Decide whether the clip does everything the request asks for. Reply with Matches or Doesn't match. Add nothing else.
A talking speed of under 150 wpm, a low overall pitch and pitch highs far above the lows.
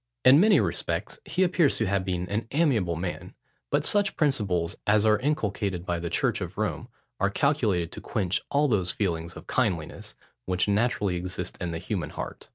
Doesn't match